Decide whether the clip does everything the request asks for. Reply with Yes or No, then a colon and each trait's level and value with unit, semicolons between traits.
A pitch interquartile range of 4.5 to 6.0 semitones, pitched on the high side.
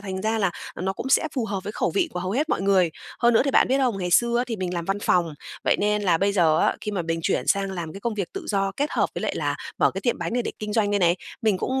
No: average, 3.9 semitones; high, 200 Hz